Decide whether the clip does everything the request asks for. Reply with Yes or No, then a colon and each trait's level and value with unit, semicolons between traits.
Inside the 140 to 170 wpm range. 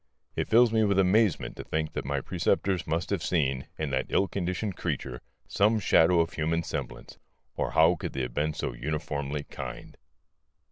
No: average, 180 wpm